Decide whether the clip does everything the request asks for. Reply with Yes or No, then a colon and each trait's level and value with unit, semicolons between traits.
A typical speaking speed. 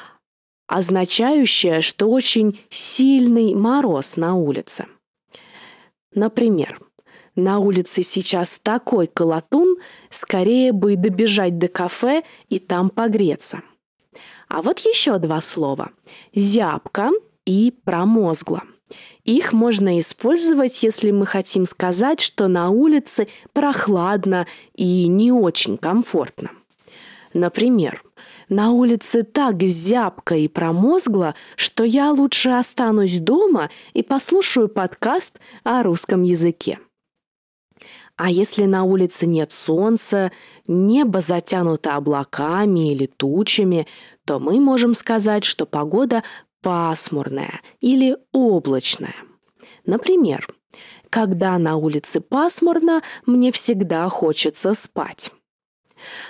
No: slow, 95 wpm